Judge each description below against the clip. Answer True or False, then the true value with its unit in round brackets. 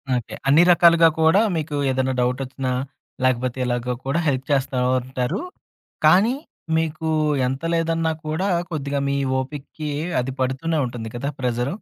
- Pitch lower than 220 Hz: True (140 Hz)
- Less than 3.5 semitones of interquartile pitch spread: False (3.9 semitones)